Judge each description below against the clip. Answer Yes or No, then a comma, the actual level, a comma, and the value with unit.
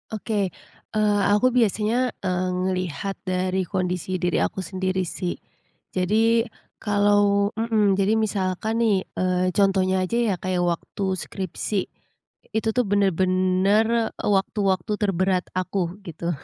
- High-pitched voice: Yes, high, 195 Hz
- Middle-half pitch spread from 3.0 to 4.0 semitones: No, narrow, 2.4 semitones